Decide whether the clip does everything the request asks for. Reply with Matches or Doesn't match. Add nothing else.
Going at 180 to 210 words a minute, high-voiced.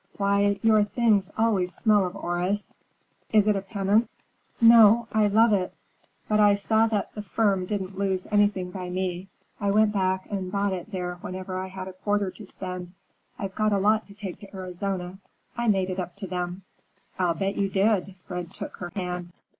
Matches